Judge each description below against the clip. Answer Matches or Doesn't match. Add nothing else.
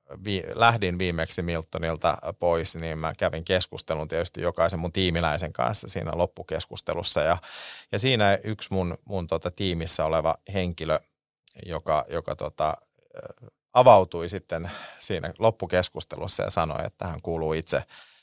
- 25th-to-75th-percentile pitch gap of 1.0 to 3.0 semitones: Matches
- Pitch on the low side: Matches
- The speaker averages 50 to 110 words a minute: Doesn't match